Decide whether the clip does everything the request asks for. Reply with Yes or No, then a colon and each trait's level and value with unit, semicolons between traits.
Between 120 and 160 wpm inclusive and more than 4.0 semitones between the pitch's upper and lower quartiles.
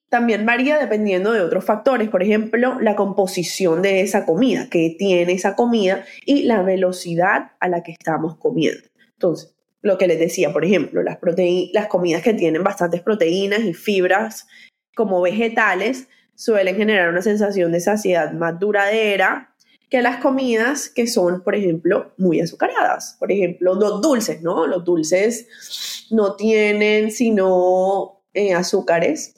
No: average, 150 wpm; average, 3.7 semitones